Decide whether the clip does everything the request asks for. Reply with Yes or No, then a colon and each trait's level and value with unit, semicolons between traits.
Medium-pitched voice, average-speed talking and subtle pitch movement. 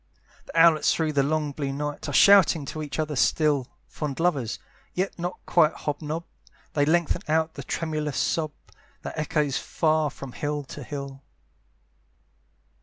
Yes: medium, 150 Hz; average, 155 wpm; narrow, 1.9 semitones